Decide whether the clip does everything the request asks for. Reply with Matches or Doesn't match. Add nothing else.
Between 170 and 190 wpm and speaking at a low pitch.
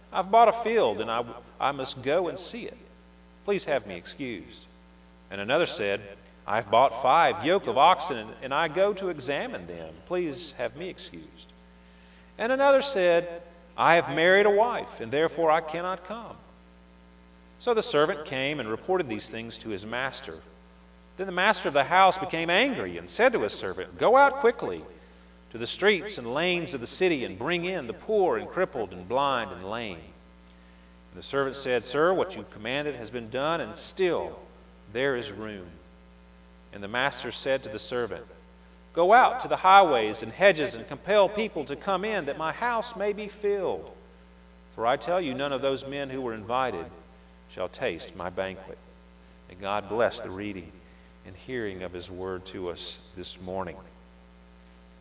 Matches